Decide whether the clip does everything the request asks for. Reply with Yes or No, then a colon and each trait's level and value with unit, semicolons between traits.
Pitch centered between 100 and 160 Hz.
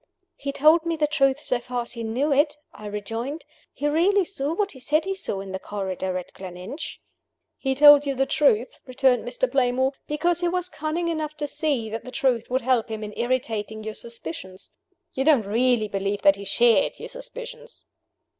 No: very high, 265 Hz